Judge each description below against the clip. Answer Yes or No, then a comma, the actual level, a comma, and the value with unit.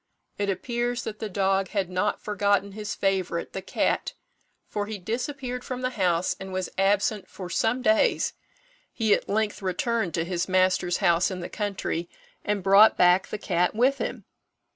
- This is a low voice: No, high, 200 Hz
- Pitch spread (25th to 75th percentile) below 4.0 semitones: Yes, average, 2.9 semitones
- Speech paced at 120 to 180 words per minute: Yes, average, 170 wpm